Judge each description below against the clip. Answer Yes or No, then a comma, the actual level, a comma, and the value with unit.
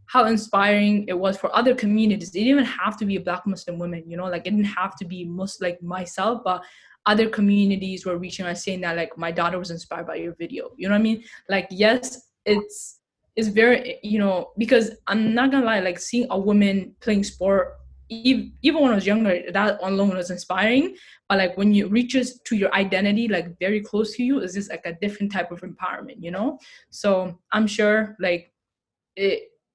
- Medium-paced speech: No, fast, 210 wpm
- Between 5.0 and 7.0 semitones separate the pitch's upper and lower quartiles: No, average, 3.5 semitones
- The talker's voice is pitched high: Yes, high, 200 Hz